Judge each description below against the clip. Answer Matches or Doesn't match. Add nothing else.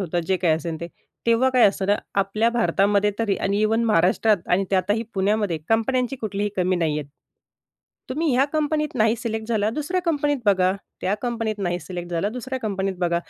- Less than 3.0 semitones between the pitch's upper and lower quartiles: Doesn't match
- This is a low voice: Doesn't match